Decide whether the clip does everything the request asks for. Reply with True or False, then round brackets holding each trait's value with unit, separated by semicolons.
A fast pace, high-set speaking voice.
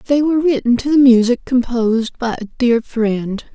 False (185 wpm; 245 Hz)